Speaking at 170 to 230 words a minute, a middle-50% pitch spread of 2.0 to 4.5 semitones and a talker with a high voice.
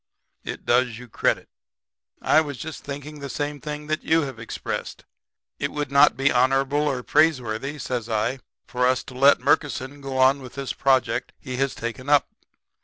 No: average, 180 wpm; narrow, 2.5 semitones; low, 135 Hz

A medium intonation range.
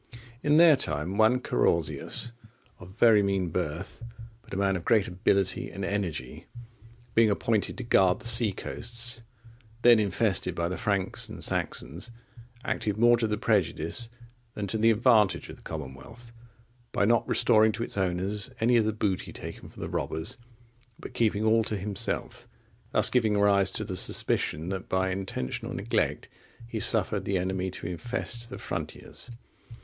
Yes: average, 3.5 semitones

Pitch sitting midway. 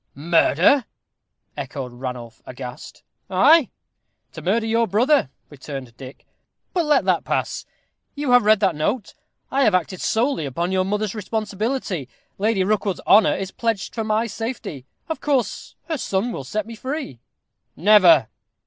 No: high, 205 Hz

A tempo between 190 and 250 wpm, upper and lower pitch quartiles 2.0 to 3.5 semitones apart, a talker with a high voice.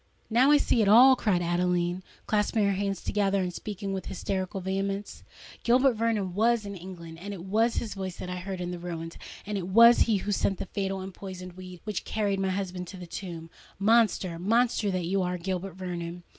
Yes: average, 195 wpm; narrow, 2.5 semitones; high, 195 Hz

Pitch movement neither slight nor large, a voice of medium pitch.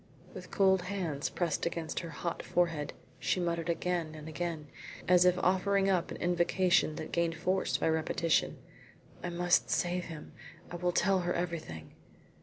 No: narrow, 1.8 semitones; medium, 175 Hz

